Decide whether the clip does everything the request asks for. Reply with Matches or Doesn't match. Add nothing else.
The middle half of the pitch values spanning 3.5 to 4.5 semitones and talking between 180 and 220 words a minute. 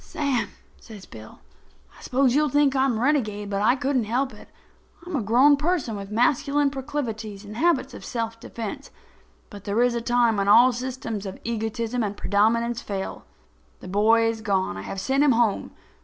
Matches